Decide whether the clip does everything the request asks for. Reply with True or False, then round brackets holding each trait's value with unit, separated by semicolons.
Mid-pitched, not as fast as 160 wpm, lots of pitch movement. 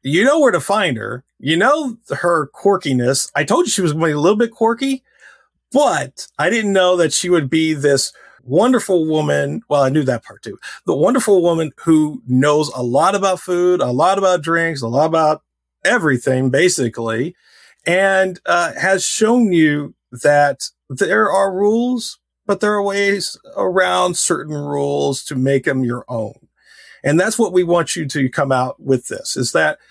False (165 Hz; 185 wpm; 6.5 semitones)